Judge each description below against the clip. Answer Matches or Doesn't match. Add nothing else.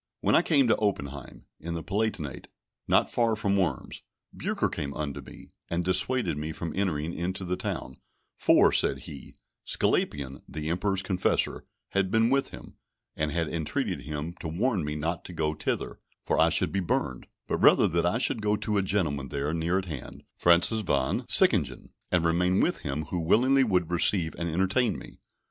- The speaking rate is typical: Matches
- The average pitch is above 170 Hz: Doesn't match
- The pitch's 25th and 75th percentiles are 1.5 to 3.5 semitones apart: Doesn't match